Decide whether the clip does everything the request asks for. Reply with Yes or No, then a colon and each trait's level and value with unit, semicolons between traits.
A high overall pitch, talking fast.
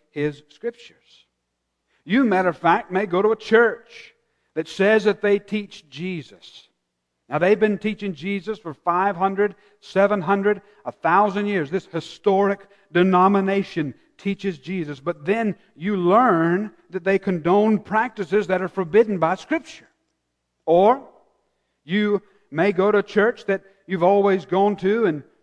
No: high, 195 Hz; slow, 135 wpm